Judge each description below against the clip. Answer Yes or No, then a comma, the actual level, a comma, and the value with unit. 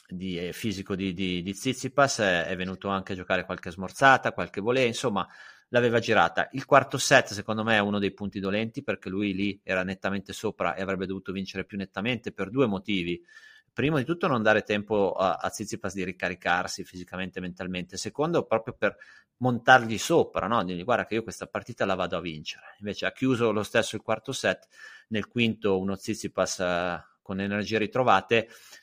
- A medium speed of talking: No, fast, 185 wpm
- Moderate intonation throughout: Yes, average, 3.4 semitones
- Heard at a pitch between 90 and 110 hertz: Yes, low, 100 Hz